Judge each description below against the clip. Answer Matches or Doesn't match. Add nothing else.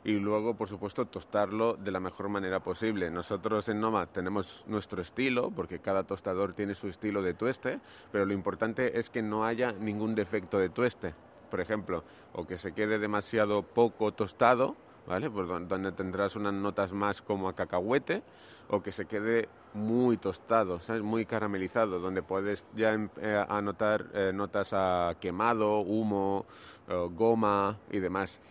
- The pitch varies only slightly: Matches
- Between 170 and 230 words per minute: Doesn't match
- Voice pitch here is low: Matches